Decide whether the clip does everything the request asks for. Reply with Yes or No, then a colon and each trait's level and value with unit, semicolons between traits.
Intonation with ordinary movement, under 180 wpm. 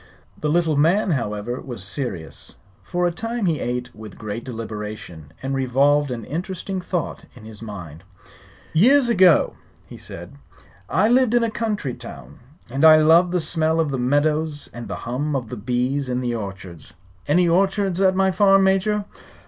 No: wide, 7.7 semitones; average, 170 wpm